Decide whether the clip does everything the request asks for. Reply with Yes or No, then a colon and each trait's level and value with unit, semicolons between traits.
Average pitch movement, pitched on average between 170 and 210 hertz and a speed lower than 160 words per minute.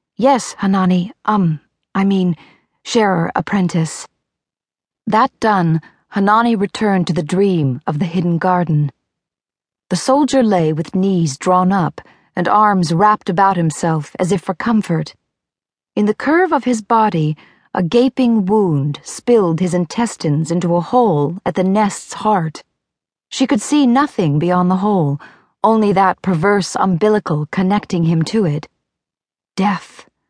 Yes: average, 3.9 semitones; high, 190 Hz; slow, 135 wpm